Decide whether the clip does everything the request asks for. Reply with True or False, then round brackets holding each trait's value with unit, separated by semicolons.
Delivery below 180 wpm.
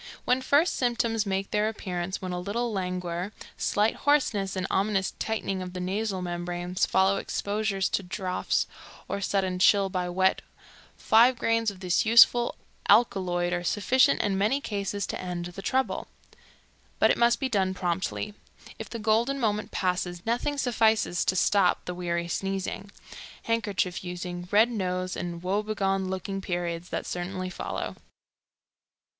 True (150 wpm)